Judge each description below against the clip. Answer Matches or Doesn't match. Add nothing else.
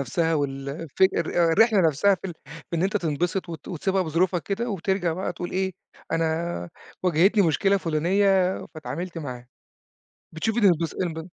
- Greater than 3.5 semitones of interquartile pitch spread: Doesn't match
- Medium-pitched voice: Matches